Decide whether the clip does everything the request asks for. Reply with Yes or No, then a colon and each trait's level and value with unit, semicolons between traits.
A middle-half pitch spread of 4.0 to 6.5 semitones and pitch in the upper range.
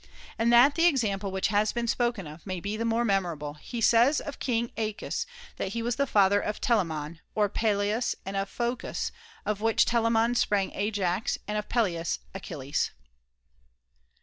No: average, 3.3 semitones; high, 210 Hz